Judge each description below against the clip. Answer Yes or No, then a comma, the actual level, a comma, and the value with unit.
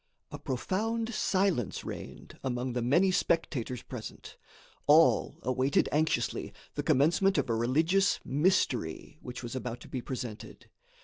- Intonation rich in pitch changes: Yes, wide, 6.3 semitones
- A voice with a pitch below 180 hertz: Yes, low, 135 Hz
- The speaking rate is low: Yes, slow, 130 wpm